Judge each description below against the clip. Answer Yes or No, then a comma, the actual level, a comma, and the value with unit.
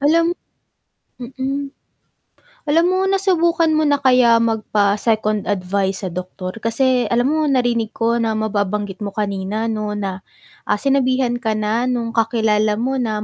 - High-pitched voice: Yes, high, 230 Hz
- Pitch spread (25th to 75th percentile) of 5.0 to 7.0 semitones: No, average, 4.0 semitones